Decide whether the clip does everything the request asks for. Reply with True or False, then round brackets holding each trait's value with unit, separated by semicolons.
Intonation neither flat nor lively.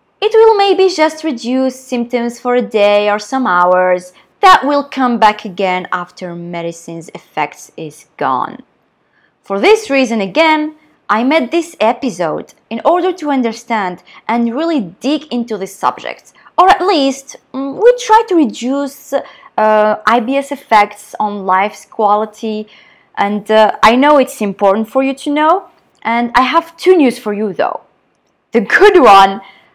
False (6.3 semitones)